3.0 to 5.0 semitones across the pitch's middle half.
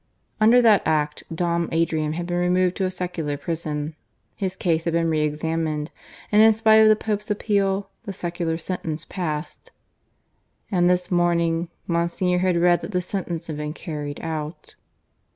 No: narrow, 2.6 semitones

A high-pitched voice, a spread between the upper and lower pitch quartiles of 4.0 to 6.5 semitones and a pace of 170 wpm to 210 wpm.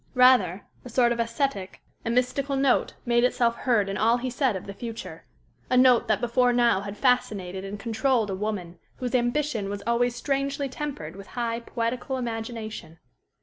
No: high, 235 Hz; average, 3.4 semitones; average, 175 wpm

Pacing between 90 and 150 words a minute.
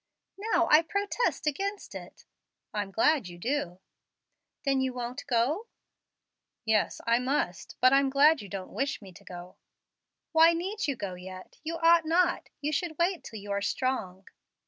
No: average, 165 wpm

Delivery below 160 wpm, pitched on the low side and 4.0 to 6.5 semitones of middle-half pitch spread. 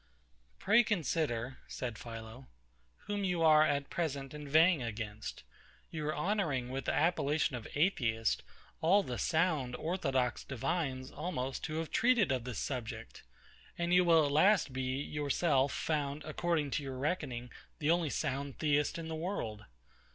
No: average, 150 wpm; medium, 145 Hz; average, 4.4 semitones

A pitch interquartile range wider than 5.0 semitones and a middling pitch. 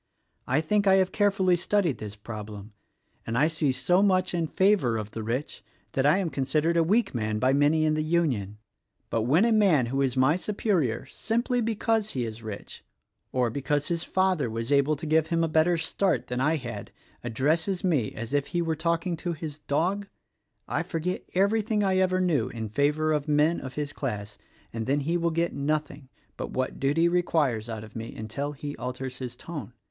Yes: wide, 5.6 semitones; medium, 150 Hz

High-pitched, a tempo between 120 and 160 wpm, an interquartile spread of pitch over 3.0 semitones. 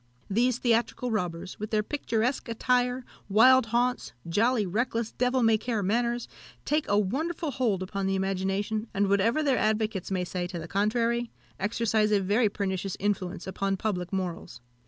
Yes: high, 215 Hz; average, 155 wpm; average, 3.7 semitones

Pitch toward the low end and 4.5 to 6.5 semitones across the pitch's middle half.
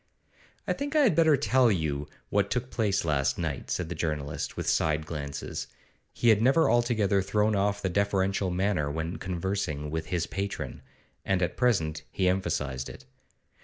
Yes: very low, 95 Hz; average, 5.1 semitones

